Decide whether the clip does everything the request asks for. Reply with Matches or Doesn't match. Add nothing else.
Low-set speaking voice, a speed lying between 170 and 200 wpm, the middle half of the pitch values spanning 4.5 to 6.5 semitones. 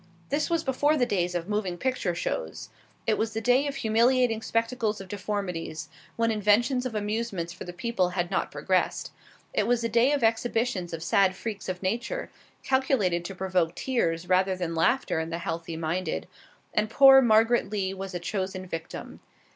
Doesn't match